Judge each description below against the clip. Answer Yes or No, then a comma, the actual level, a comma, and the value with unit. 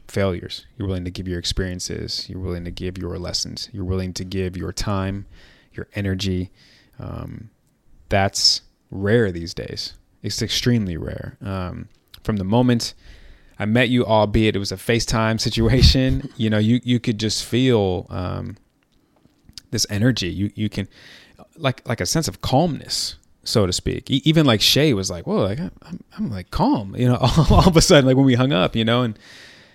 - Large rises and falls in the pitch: No, average, 4.6 semitones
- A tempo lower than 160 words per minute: No, average, 180 wpm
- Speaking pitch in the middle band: No, low, 105 Hz